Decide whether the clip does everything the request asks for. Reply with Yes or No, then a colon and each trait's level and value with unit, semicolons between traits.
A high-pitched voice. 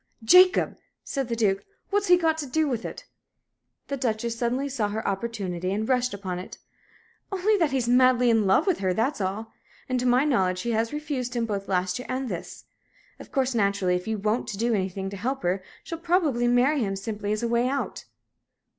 Yes: high, 235 Hz